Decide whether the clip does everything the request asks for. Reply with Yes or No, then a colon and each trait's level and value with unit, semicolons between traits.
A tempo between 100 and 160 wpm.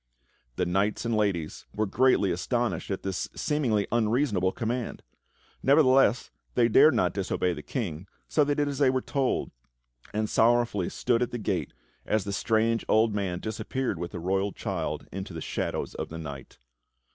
No: average, 170 wpm